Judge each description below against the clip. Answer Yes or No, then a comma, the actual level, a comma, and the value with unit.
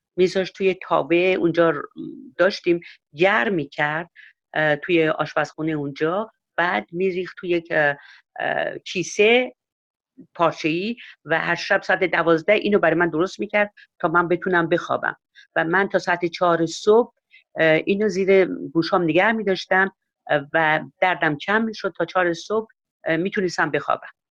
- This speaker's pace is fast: No, average, 125 wpm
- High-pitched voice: No, medium, 175 Hz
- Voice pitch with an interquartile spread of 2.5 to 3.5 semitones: Yes, average, 3.1 semitones